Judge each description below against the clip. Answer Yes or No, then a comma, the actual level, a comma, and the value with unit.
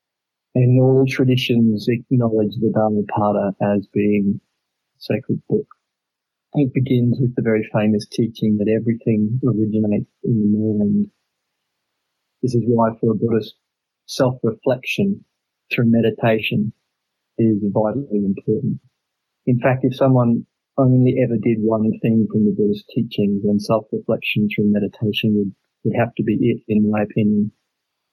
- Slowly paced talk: Yes, slow, 130 wpm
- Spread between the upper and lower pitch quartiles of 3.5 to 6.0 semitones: No, average, 2.9 semitones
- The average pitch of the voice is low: Yes, low, 110 Hz